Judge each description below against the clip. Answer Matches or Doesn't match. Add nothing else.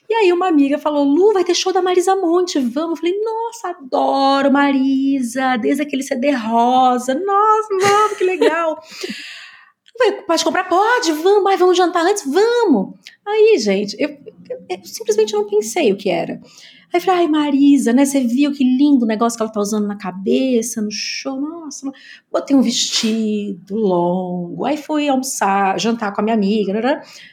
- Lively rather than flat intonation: Matches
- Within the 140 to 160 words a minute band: Doesn't match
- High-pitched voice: Matches